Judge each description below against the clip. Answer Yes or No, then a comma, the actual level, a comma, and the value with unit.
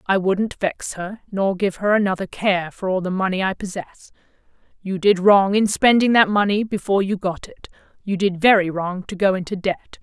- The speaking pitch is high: Yes, high, 195 Hz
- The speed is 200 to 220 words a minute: Yes, fast, 205 wpm